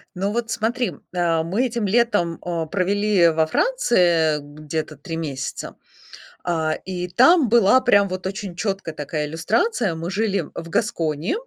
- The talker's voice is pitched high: No, medium, 180 Hz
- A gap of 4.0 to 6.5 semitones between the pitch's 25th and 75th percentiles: Yes, average, 5.2 semitones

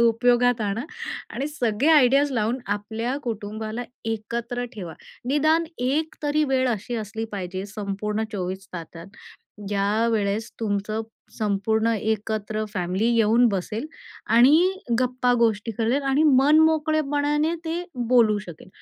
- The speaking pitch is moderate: No, high, 225 Hz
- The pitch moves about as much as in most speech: Yes, average, 4.0 semitones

